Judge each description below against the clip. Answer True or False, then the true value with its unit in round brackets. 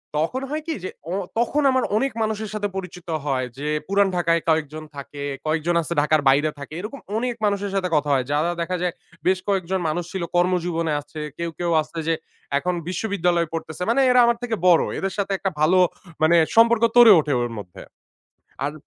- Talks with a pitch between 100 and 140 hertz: False (175 Hz)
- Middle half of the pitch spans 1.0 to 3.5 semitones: False (4.5 semitones)